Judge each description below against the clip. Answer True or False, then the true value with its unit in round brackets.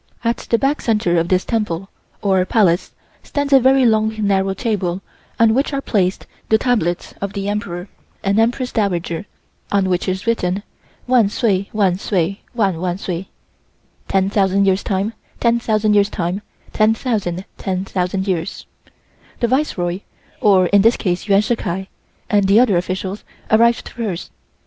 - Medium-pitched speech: False (200 Hz)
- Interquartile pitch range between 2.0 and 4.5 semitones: True (3.3 semitones)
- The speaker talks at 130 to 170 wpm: True (150 wpm)